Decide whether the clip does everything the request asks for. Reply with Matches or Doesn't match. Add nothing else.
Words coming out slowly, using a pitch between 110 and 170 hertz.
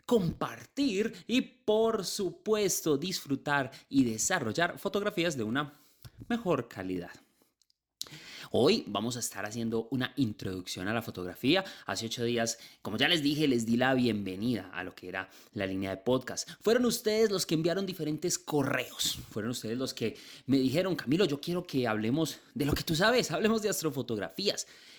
Doesn't match